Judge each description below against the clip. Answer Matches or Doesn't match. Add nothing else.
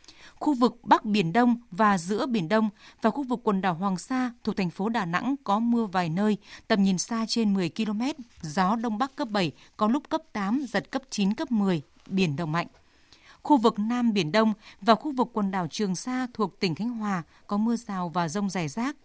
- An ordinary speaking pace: Matches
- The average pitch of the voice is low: Doesn't match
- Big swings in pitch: Doesn't match